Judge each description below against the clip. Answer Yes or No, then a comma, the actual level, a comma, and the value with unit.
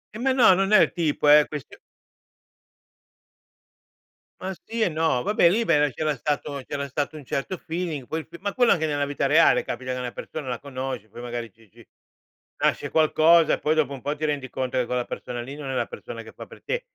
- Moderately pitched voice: Yes, medium, 150 Hz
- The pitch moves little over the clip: No, average, 4.3 semitones